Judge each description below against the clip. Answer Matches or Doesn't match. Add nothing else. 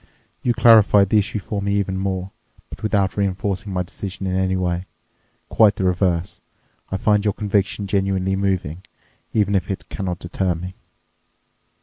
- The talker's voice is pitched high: Doesn't match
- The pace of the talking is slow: Doesn't match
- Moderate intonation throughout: Doesn't match